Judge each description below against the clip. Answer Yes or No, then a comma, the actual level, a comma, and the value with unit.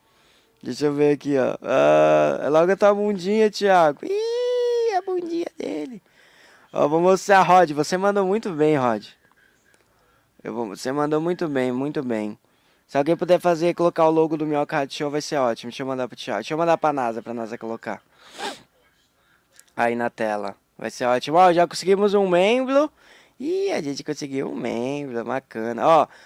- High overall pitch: No, medium, 150 Hz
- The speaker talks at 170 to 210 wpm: Yes, average, 180 wpm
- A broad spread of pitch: Yes, wide, 7.5 semitones